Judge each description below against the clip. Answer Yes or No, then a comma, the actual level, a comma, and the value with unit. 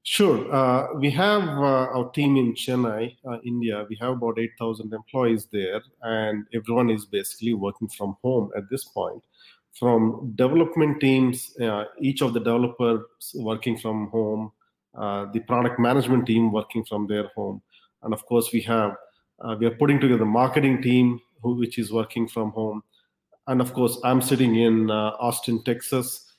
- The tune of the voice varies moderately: No, narrow, 2.3 semitones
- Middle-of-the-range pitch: No, low, 120 Hz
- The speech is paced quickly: No, average, 170 wpm